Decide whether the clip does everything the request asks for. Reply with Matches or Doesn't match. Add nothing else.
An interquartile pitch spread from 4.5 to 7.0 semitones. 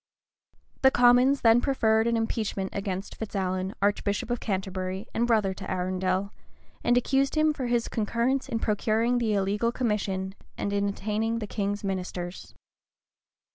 Doesn't match